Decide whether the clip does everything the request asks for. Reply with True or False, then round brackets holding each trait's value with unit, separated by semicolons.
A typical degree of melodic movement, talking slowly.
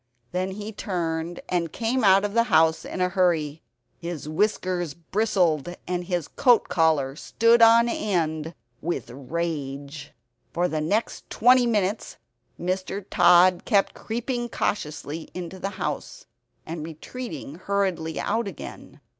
True (4.3 semitones; 130 wpm)